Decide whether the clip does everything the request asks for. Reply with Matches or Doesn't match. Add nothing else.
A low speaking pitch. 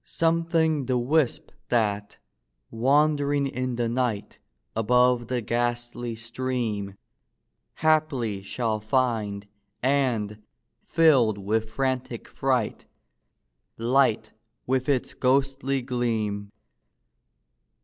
Matches